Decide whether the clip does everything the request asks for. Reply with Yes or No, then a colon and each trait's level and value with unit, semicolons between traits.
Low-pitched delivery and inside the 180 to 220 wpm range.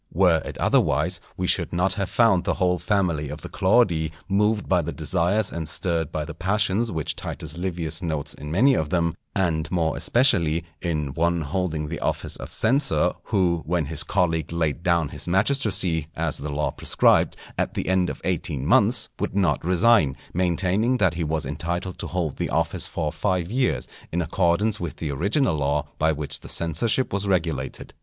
Yes: very low, 85 Hz; average, 185 wpm